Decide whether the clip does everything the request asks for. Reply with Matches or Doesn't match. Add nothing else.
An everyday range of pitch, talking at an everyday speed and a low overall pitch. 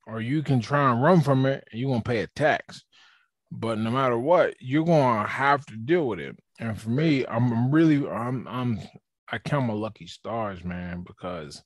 Doesn't match